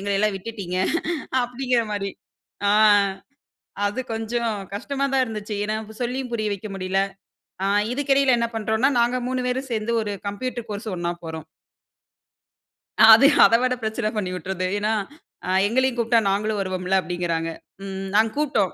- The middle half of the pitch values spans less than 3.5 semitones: No, average, 3.8 semitones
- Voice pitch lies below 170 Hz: No, high, 220 Hz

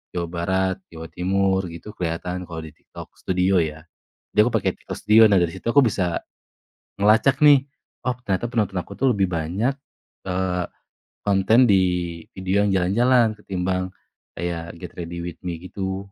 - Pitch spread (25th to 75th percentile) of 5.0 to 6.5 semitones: No, average, 3.1 semitones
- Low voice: Yes, very low, 95 Hz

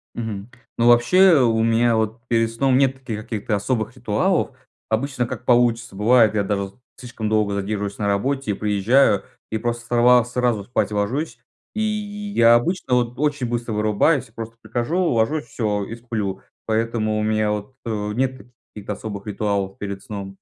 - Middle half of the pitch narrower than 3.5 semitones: Yes, average, 2.9 semitones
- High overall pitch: No, low, 115 Hz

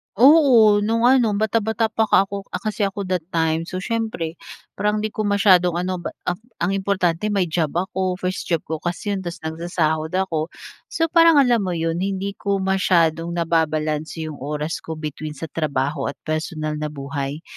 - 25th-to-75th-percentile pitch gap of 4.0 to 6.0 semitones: Yes, average, 4.3 semitones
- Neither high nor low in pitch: Yes, medium, 180 Hz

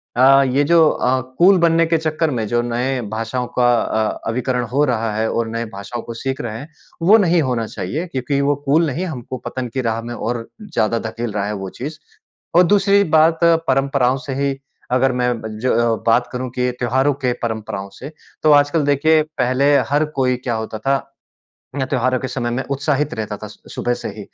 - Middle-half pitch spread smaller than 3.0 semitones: No, average, 3.5 semitones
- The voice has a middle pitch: No, low, 130 Hz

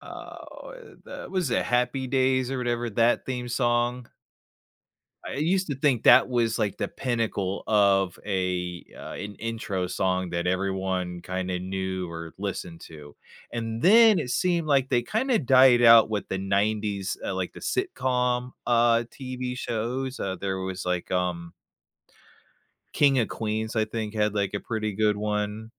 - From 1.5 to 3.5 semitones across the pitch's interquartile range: No, average, 4.8 semitones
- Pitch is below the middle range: Yes, low, 110 Hz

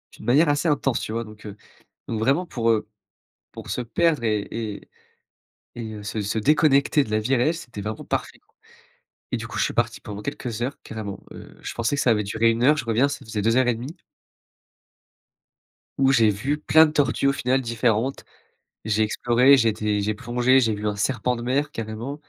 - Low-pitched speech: Yes, low, 115 Hz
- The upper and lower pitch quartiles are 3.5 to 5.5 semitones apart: Yes, average, 3.9 semitones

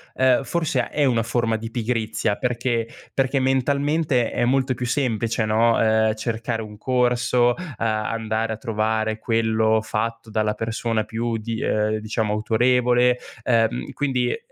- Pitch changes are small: Yes, narrow, 2.2 semitones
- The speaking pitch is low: Yes, low, 115 Hz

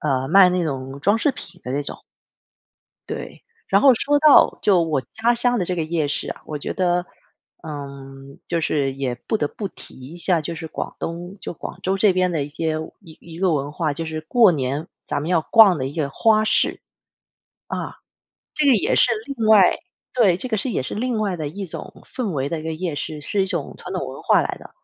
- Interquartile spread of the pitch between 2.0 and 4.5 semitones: No, wide, 5.6 semitones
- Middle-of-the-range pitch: Yes, medium, 170 Hz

